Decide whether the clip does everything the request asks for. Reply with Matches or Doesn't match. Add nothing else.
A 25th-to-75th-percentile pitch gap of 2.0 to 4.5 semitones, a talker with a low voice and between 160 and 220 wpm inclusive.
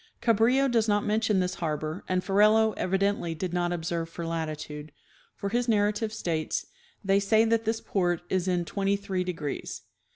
Doesn't match